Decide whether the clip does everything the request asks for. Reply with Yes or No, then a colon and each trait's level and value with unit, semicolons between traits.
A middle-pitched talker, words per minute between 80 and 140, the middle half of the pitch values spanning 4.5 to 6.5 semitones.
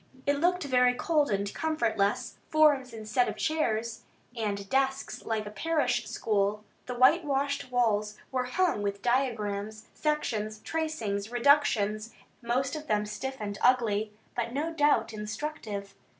No: high, 245 Hz; slow, 135 wpm; average, 5.1 semitones